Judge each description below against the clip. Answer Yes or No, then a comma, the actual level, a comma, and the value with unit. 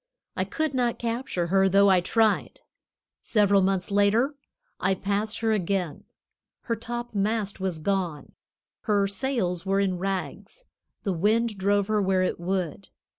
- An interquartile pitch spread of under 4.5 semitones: Yes, average, 2.9 semitones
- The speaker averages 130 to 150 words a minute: Yes, average, 140 wpm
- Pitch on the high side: Yes, high, 200 Hz